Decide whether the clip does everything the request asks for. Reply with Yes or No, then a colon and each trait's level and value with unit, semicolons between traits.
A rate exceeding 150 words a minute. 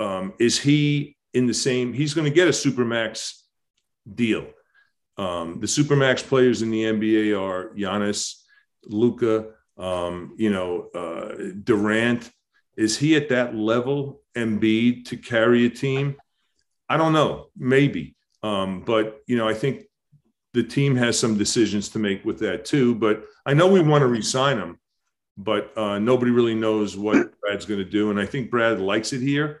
Yes: average, 170 wpm